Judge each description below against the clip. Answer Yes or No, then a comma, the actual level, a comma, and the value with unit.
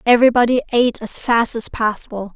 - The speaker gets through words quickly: No, average, 155 wpm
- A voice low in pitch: No, high, 230 Hz